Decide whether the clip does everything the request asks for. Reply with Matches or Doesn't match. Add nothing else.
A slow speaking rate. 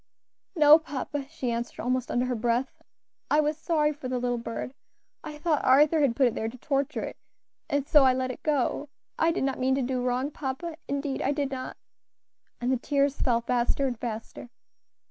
Doesn't match